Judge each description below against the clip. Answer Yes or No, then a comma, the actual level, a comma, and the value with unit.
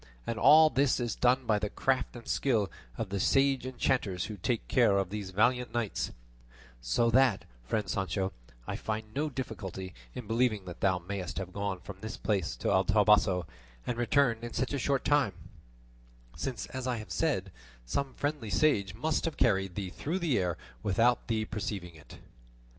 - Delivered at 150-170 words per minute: No, average, 180 wpm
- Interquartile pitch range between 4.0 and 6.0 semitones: Yes, average, 4.9 semitones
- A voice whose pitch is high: No, low, 110 Hz